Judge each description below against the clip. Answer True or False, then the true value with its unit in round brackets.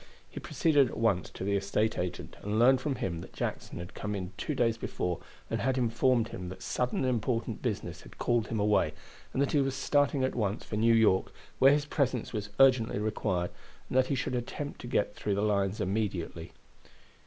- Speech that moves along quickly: True (210 wpm)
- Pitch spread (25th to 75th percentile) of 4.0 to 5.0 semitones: True (4.6 semitones)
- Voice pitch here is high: False (110 Hz)